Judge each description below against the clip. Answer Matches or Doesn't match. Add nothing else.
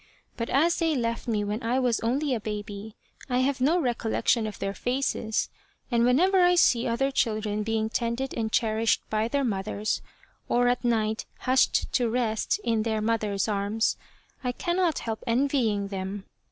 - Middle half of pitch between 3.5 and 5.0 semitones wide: Doesn't match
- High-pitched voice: Matches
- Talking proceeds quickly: Doesn't match